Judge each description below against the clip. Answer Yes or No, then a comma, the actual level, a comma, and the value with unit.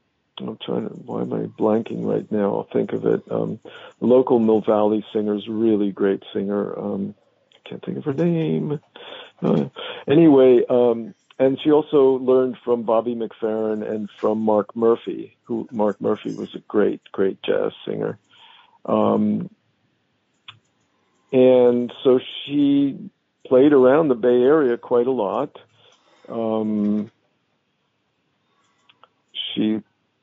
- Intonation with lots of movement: Yes, wide, 6.5 semitones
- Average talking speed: No, slow, 130 wpm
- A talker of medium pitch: No, low, 120 Hz